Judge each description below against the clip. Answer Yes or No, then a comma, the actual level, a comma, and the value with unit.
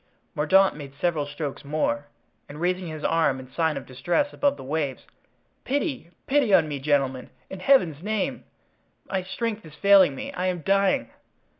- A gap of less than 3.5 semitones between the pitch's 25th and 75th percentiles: No, average, 5.2 semitones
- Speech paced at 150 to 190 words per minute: Yes, average, 165 wpm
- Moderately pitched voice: Yes, medium, 165 Hz